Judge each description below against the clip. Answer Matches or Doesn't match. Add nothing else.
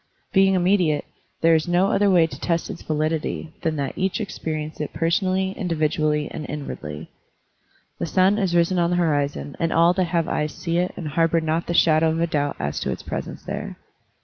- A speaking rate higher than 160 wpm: Matches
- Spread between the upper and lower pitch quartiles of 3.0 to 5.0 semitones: Doesn't match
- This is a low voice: Doesn't match